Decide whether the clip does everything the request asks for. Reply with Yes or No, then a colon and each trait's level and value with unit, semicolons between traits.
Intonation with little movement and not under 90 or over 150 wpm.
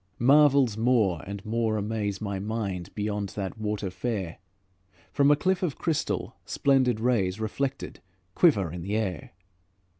No: average, 4.3 semitones; average, 140 wpm